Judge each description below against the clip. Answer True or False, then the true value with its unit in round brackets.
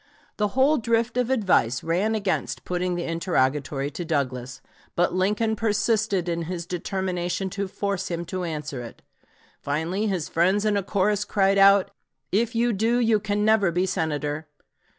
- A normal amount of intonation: True (4.0 semitones)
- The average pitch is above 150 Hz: True (190 Hz)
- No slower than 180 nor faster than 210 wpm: False (160 wpm)